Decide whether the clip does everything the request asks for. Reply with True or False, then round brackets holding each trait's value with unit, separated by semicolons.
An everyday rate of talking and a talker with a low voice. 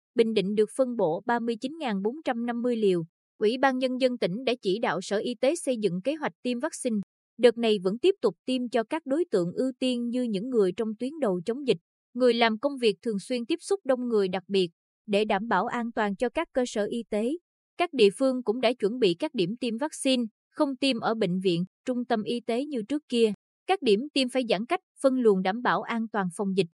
False (235 wpm; 235 Hz)